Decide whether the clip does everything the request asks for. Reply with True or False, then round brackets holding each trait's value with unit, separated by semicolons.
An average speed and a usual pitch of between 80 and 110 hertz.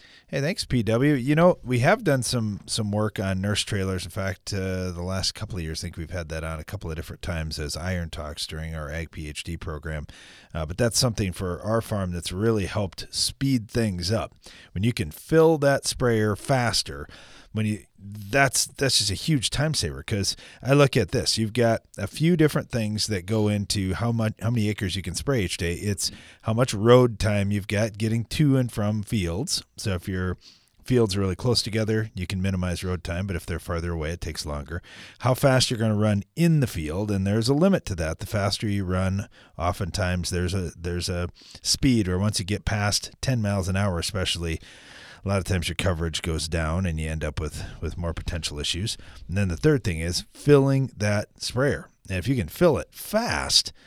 False (215 wpm; 100 Hz)